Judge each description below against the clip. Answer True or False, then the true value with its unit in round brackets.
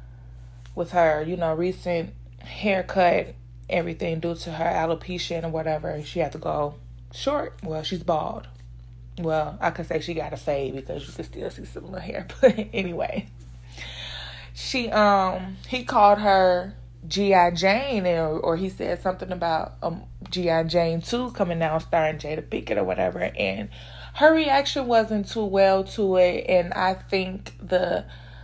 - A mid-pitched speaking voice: True (170 Hz)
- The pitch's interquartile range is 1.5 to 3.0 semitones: False (4.0 semitones)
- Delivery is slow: False (160 wpm)